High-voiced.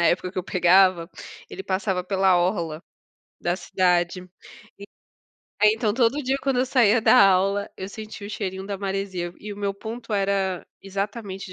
Yes: high, 195 Hz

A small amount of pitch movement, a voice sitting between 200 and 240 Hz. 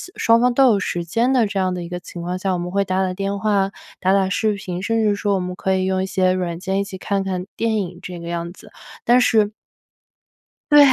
No: narrow, 2.3 semitones; high, 190 Hz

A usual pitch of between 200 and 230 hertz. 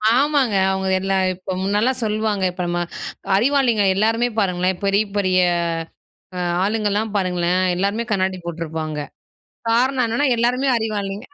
Yes: high, 205 Hz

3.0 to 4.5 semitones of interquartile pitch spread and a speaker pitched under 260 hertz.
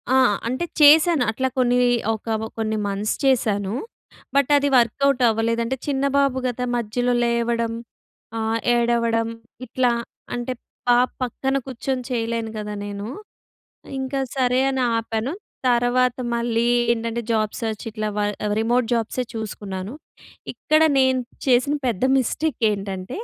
No: narrow, 2.6 semitones; high, 235 Hz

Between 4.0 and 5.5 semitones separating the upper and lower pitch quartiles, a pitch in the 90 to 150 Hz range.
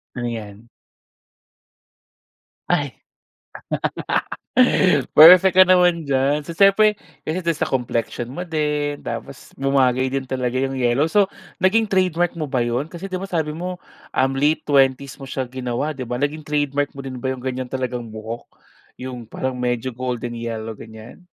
Yes: average, 4.5 semitones; low, 135 Hz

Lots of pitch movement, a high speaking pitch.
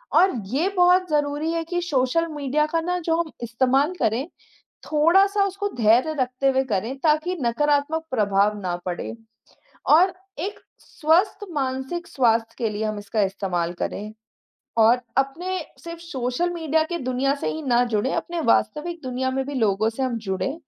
Yes: wide, 6.1 semitones; very high, 275 Hz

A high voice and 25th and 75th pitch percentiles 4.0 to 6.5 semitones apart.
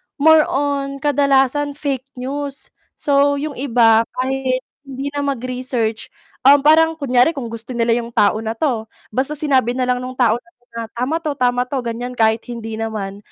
No: very high, 255 Hz; average, 3.3 semitones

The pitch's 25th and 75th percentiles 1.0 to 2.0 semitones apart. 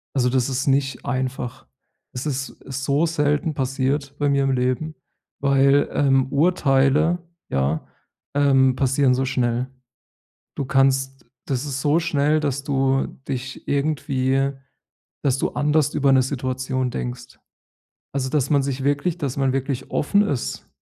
Yes: narrow, 1.7 semitones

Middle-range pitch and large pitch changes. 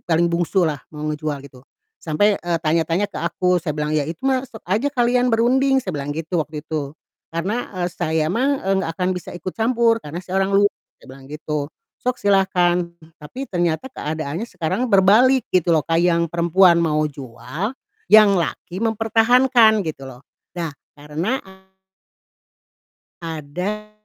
Yes: medium, 175 Hz; wide, 5.7 semitones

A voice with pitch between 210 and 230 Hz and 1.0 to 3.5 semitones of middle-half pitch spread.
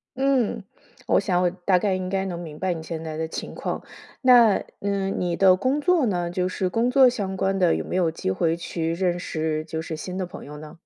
No: medium, 185 Hz; average, 3.0 semitones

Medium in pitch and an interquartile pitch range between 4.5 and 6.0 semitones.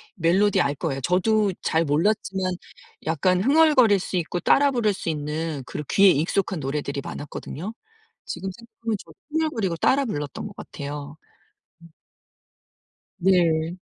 Yes: medium, 180 Hz; average, 5.3 semitones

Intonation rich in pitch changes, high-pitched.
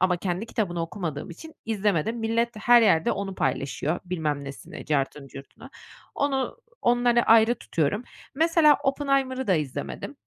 Yes: wide, 7.2 semitones; high, 205 Hz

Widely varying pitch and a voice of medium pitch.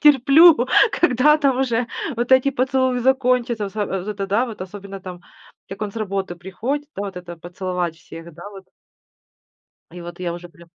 No: wide, 6.1 semitones; high, 205 Hz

